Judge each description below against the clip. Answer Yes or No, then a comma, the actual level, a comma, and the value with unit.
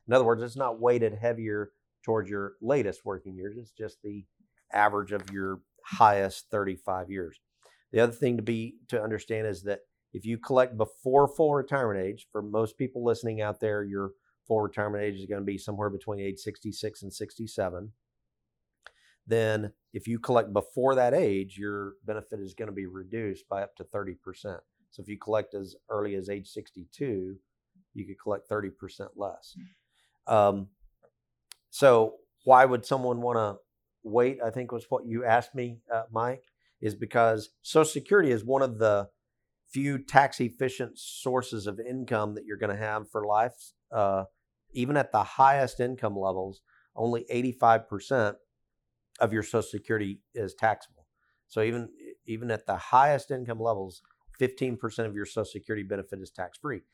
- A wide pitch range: No, average, 3.1 semitones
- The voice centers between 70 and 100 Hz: No, low, 110 Hz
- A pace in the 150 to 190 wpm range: Yes, average, 170 wpm